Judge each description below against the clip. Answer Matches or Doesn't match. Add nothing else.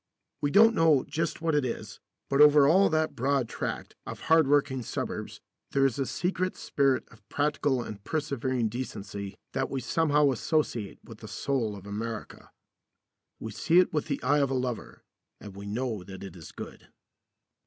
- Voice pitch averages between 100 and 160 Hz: Matches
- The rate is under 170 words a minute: Doesn't match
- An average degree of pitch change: Matches